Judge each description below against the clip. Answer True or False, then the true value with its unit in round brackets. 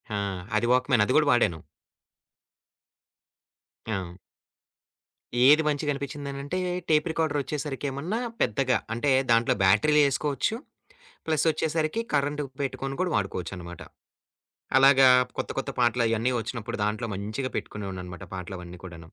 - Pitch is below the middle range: True (130 Hz)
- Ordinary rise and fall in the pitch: False (5.9 semitones)